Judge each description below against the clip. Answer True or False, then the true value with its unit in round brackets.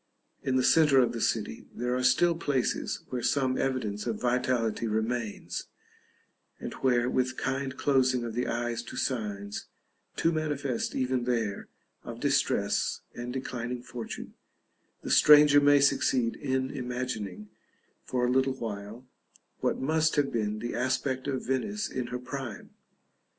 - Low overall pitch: True (125 Hz)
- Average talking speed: True (145 wpm)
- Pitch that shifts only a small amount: True (2.1 semitones)